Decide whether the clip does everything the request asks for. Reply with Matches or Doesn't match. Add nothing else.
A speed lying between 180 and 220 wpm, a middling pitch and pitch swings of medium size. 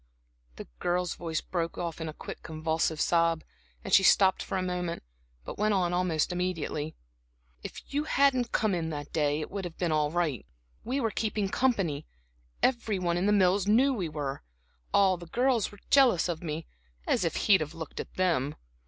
Matches